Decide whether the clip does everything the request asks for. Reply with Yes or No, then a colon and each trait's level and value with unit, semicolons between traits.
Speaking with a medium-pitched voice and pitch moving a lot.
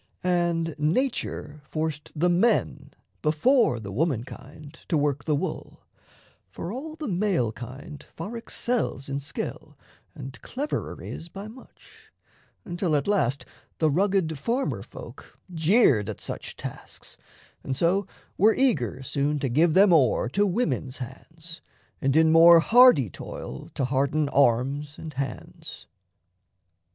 Yes: medium, 160 Hz; wide, 5.8 semitones